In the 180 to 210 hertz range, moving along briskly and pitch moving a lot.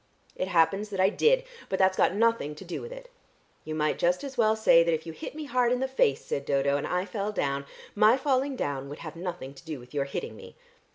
Yes: medium, 185 Hz; fast, 250 wpm; wide, 7.3 semitones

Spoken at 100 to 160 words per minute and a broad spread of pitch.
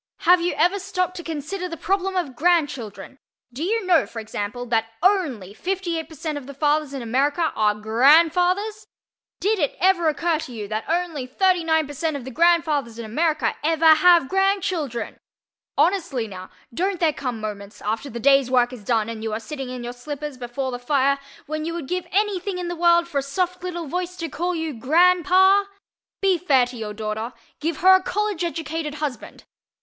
No: average, 185 wpm; wide, 6.0 semitones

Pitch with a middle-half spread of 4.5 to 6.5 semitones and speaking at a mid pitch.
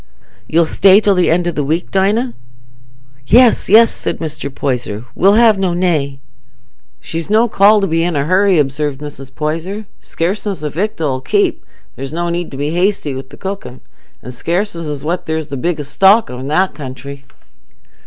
Yes: wide, 5.4 semitones; medium, 165 Hz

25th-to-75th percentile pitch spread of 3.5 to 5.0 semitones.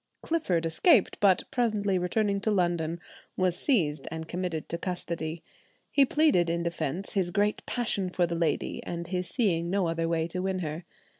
No: average, 3.1 semitones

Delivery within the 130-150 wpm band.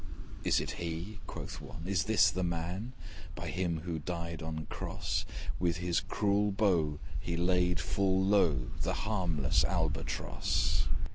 Yes: average, 140 wpm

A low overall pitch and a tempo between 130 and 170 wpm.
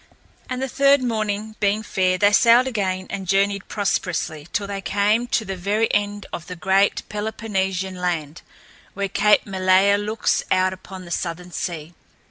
No: high, 200 Hz; average, 160 wpm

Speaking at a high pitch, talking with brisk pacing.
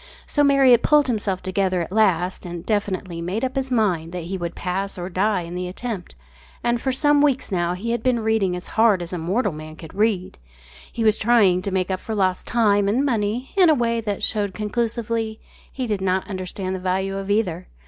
Yes: high, 205 Hz; fast, 210 wpm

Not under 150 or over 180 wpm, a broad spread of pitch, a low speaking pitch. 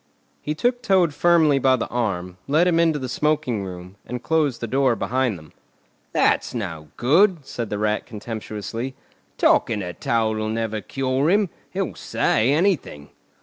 Yes: average, 155 wpm; wide, 6.0 semitones; low, 125 Hz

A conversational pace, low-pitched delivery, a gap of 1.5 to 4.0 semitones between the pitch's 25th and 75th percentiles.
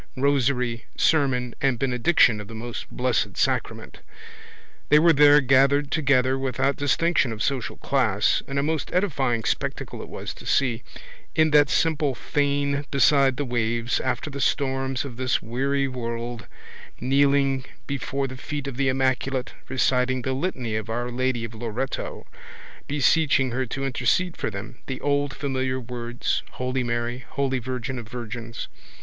Yes: average, 150 wpm; low, 130 Hz; narrow, 2.5 semitones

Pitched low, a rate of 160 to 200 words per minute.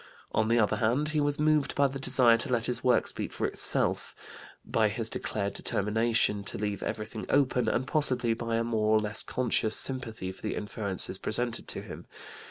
Yes: low, 115 Hz; average, 190 wpm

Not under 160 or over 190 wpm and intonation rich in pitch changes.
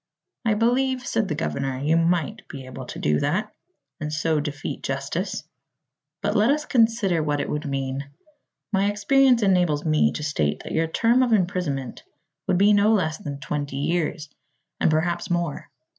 Yes: average, 170 wpm; wide, 6.2 semitones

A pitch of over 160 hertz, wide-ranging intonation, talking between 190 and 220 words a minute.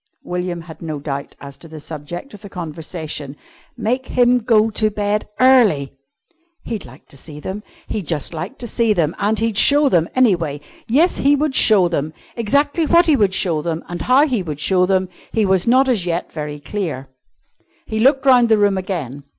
Yes: high, 190 Hz; wide, 6.8 semitones; average, 195 wpm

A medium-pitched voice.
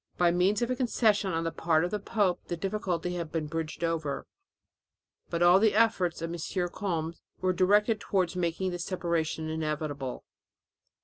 Yes: medium, 175 Hz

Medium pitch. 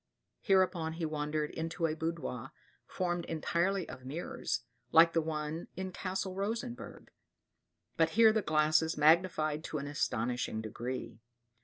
Yes: medium, 160 Hz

